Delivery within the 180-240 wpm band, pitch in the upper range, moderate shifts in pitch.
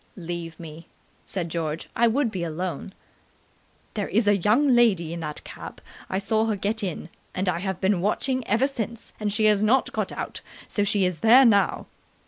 Yes: average, 190 wpm; high, 200 Hz; average, 4.4 semitones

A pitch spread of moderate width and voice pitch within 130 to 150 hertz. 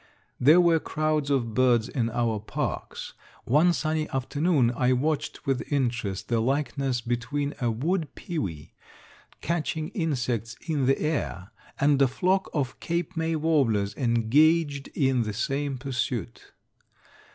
Yes: average, 4.6 semitones; low, 135 Hz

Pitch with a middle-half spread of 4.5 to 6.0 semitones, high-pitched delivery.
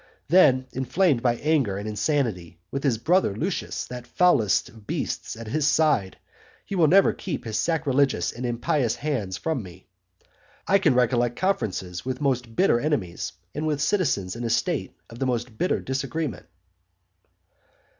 No: wide, 5.5 semitones; low, 130 Hz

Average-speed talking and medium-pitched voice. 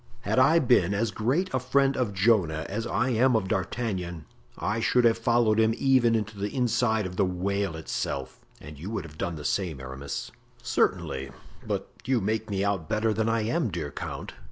No: average, 190 wpm; low, 110 Hz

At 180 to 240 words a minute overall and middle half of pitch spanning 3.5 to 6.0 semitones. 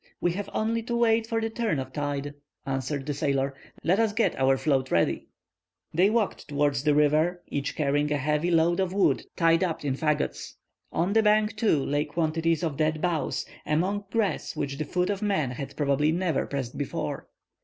Yes: average, 190 wpm; average, 5.2 semitones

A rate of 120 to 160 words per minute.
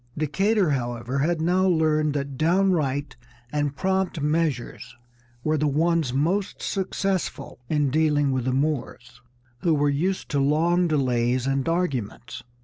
Yes: slow, 135 wpm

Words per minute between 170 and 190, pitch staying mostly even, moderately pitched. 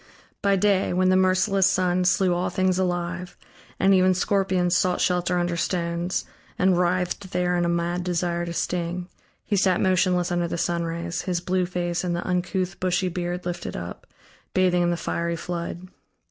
Yes: average, 175 wpm; narrow, 1.1 semitones; medium, 180 Hz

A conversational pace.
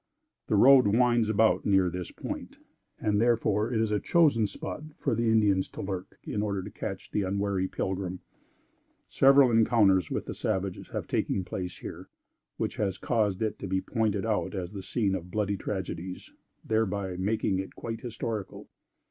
Yes: average, 170 wpm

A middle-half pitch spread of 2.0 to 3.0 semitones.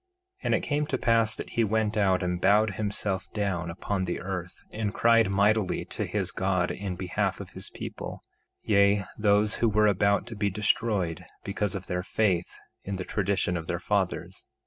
Yes: narrow, 2.5 semitones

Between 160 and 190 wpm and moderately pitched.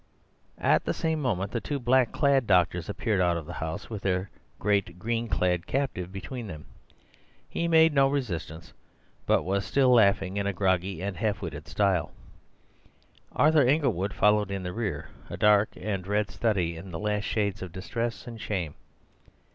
No: average, 170 wpm; low, 100 Hz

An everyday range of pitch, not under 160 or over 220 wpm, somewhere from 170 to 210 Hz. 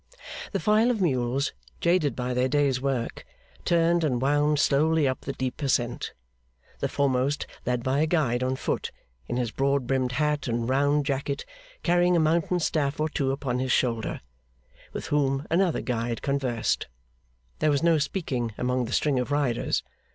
No: average, 3.3 semitones; average, 165 wpm; medium, 140 Hz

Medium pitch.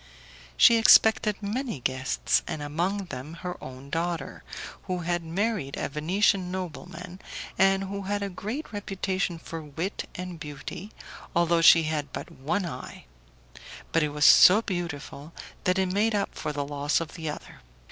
Yes: medium, 175 Hz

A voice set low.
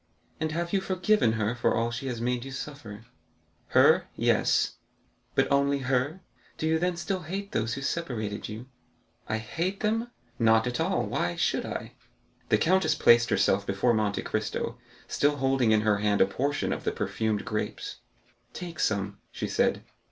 Yes: low, 125 Hz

